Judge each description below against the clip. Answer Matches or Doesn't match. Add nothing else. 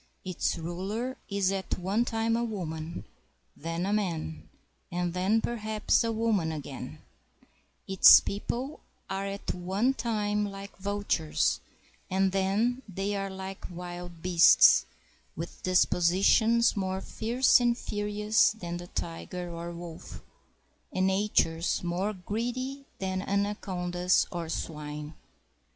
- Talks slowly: Matches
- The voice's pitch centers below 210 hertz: Matches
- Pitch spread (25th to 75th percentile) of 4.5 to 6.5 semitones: Doesn't match